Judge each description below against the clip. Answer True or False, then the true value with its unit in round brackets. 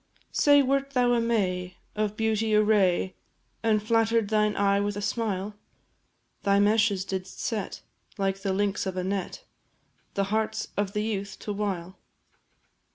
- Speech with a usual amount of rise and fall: False (2.2 semitones)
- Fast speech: False (155 wpm)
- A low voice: False (205 Hz)